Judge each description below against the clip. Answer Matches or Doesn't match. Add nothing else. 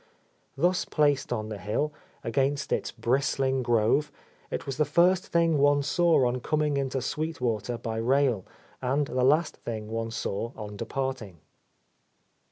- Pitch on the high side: Doesn't match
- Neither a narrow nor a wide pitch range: Matches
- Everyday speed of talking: Matches